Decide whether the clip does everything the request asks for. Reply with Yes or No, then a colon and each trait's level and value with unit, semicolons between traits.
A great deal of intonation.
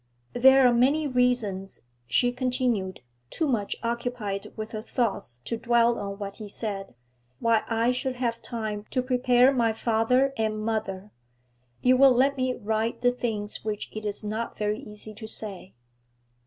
No: average, 2.8 semitones